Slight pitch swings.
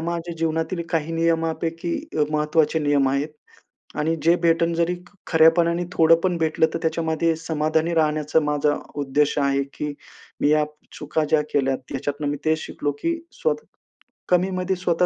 Yes: narrow, 2.0 semitones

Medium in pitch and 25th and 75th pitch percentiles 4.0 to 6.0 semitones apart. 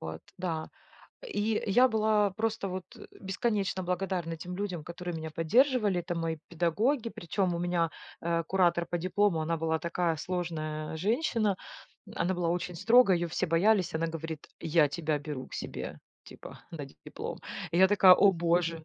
No: medium, 175 Hz; average, 3.3 semitones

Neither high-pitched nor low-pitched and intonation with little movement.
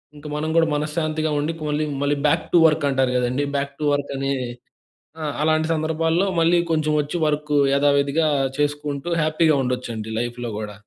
Yes: medium, 150 Hz; narrow, 2.0 semitones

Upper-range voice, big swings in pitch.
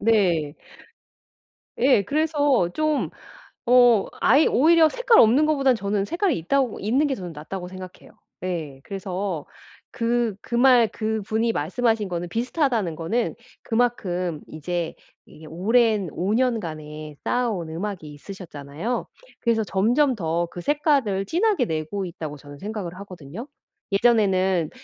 Yes: high, 205 Hz; wide, 6.1 semitones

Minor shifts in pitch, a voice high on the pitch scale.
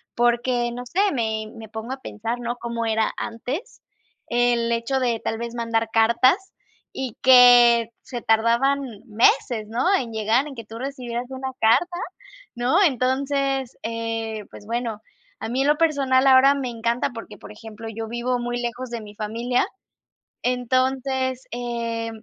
Yes: narrow, 2.3 semitones; high, 240 Hz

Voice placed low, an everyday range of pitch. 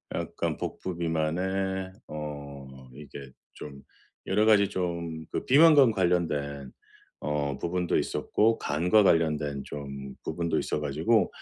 Yes: very low, 80 Hz; average, 4.6 semitones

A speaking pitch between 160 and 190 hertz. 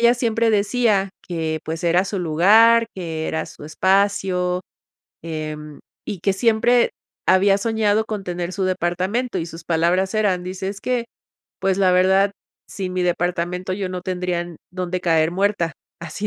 Yes: medium, 185 Hz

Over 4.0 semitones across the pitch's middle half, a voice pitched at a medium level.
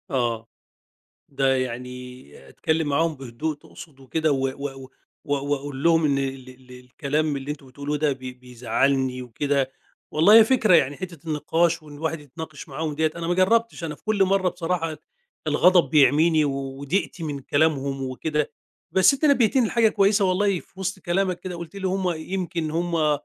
Yes: average, 4.4 semitones; medium, 155 Hz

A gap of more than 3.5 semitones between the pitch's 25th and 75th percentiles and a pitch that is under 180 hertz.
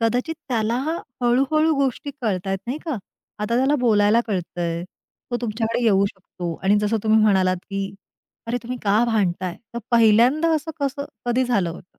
No: average, 4.1 semitones; high, 225 Hz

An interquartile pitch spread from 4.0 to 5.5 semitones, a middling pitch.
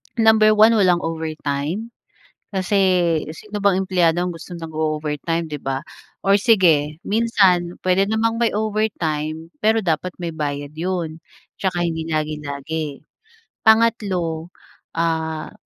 Yes: average, 4.4 semitones; medium, 170 Hz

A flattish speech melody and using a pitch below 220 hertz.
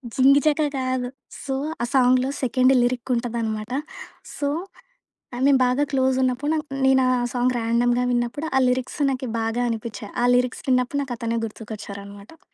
No: narrow, 2.1 semitones; very high, 250 Hz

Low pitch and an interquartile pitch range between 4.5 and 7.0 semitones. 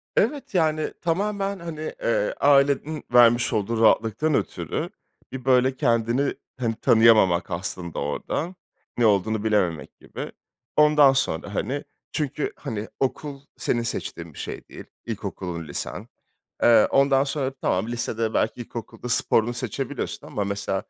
Yes: low, 120 Hz; average, 5.0 semitones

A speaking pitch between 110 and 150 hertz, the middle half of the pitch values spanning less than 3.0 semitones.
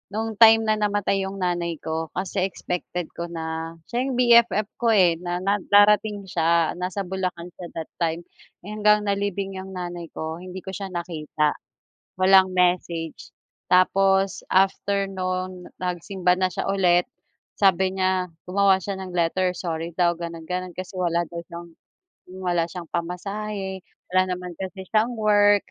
No: medium, 185 Hz; narrow, 2.4 semitones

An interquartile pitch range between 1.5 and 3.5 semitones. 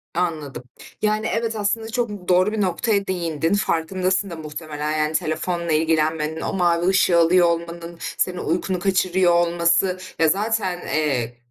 Yes: average, 2.9 semitones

